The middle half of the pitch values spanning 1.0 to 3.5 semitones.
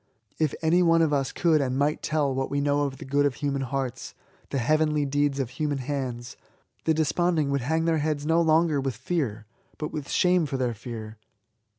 Yes: average, 2.9 semitones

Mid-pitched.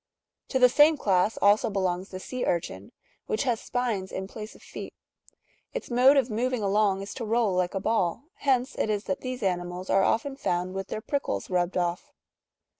No: high, 210 Hz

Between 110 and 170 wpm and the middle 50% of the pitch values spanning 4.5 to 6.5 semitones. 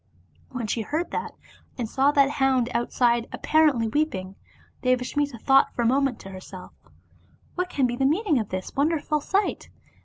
No: average, 165 wpm; average, 3.8 semitones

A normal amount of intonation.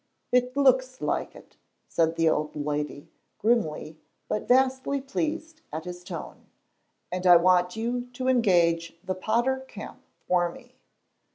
No: wide, 7.4 semitones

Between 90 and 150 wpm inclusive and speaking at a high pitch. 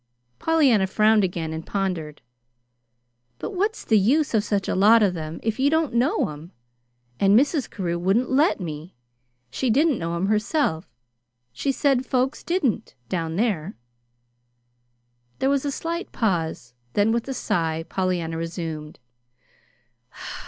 Yes: average, 140 wpm; high, 205 Hz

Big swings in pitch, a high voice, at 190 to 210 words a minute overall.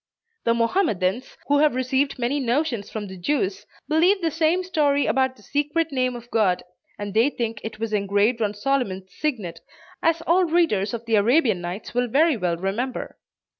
No: wide, 6.1 semitones; high, 245 Hz; average, 175 wpm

